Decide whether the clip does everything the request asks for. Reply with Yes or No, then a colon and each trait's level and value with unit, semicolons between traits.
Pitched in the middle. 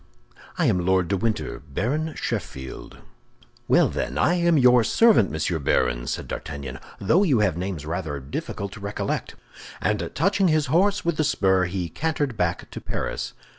No: low, 100 Hz